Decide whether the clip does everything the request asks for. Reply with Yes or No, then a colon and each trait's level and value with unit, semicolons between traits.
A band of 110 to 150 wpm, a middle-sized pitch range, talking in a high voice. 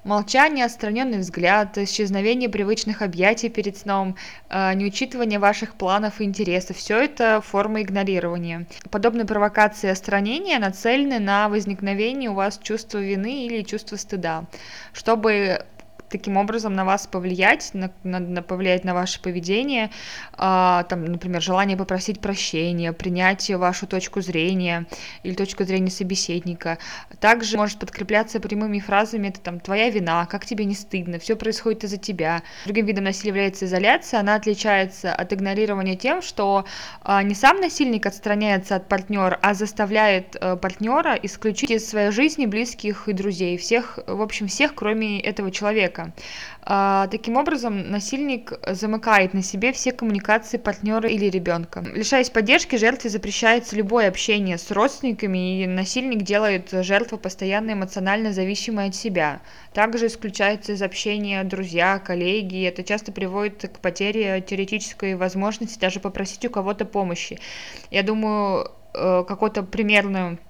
No: average, 135 wpm; narrow, 2.3 semitones; high, 205 Hz